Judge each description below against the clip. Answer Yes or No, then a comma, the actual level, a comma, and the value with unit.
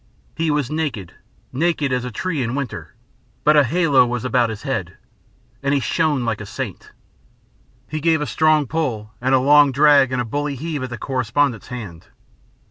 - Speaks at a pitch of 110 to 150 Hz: Yes, medium, 140 Hz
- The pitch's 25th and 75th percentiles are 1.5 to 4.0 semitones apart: Yes, average, 3.6 semitones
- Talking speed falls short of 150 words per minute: No, average, 185 wpm